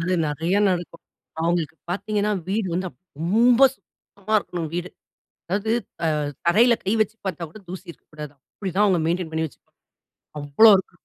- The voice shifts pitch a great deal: No, average, 3.8 semitones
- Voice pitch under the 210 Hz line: Yes, medium, 185 Hz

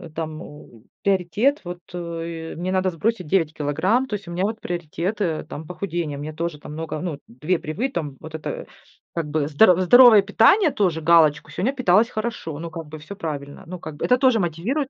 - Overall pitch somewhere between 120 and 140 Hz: No, medium, 170 Hz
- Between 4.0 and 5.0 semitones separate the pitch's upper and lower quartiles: Yes, average, 4.5 semitones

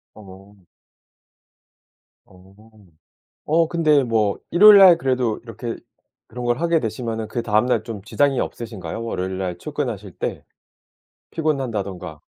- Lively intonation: Yes, wide, 5.9 semitones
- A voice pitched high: No, low, 115 Hz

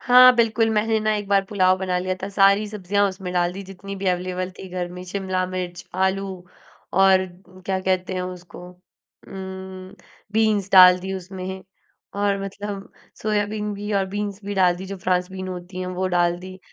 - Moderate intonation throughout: No, narrow, 1.6 semitones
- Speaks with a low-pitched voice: No, high, 190 Hz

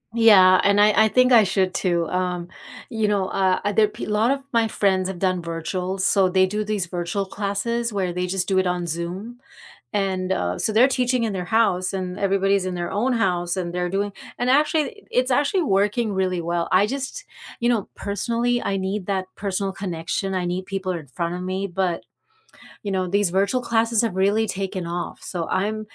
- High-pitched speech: Yes, high, 195 Hz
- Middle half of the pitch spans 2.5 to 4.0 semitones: Yes, average, 2.9 semitones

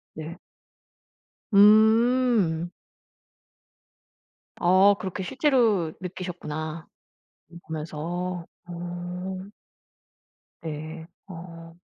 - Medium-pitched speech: Yes, medium, 175 Hz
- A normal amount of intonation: Yes, average, 3.1 semitones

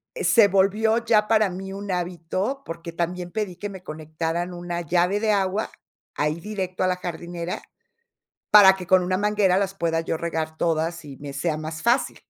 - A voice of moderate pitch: Yes, medium, 180 Hz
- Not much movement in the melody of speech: No, average, 3.2 semitones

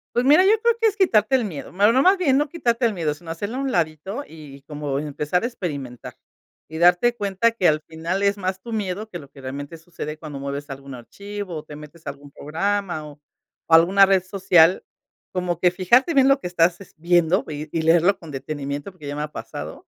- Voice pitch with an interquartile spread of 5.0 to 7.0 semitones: Yes, wide, 5.4 semitones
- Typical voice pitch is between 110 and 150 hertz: No, medium, 175 Hz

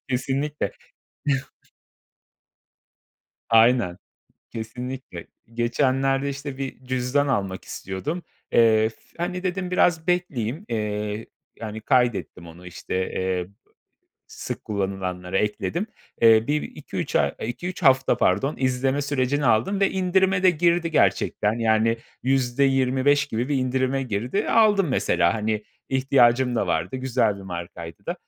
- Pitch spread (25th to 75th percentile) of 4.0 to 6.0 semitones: Yes, average, 4.8 semitones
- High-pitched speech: No, low, 125 Hz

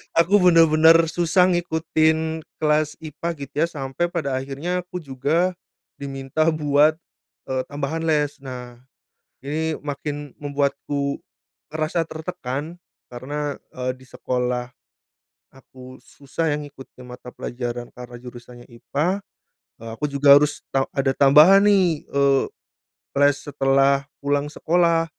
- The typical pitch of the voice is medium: Yes, medium, 145 Hz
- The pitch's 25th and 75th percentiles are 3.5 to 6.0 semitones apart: No, average, 3.1 semitones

